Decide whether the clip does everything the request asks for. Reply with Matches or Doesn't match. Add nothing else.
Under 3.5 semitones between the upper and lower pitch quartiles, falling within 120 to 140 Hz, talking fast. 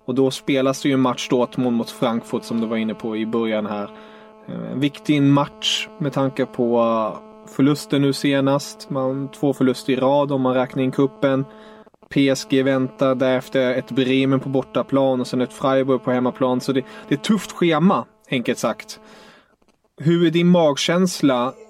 Doesn't match